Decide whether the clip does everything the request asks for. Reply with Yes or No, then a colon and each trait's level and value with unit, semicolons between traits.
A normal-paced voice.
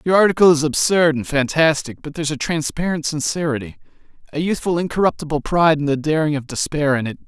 Yes: average, 180 wpm